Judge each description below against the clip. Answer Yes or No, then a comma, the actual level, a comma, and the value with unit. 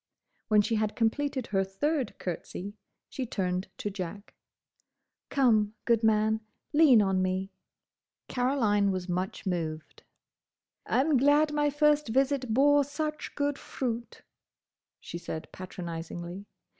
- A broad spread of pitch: Yes, wide, 6.6 semitones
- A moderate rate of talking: No, slow, 120 wpm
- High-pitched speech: Yes, high, 220 Hz